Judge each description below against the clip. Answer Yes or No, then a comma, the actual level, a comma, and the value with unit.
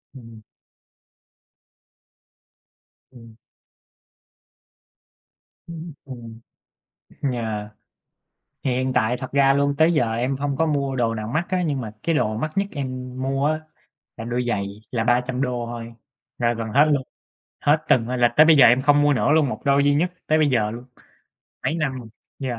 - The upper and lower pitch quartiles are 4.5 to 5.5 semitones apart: No, average, 3.5 semitones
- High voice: No, low, 130 Hz